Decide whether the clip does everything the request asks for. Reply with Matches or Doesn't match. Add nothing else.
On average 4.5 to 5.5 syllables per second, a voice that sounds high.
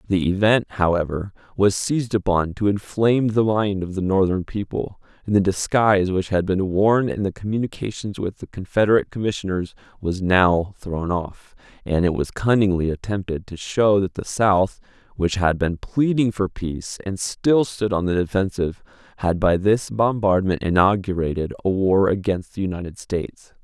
Doesn't match